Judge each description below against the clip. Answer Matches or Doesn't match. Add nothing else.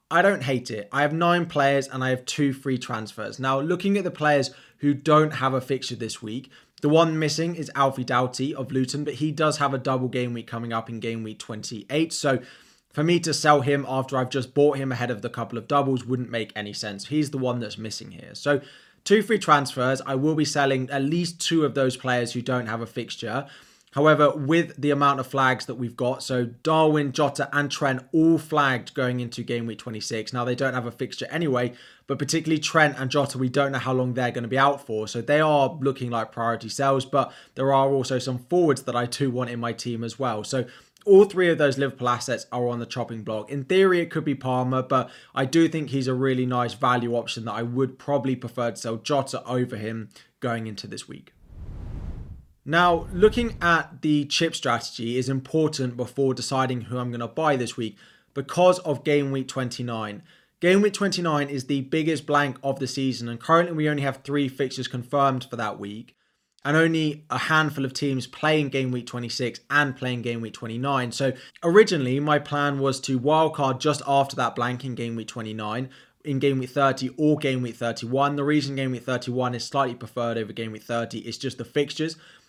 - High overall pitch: Doesn't match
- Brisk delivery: Matches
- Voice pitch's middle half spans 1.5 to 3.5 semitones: Matches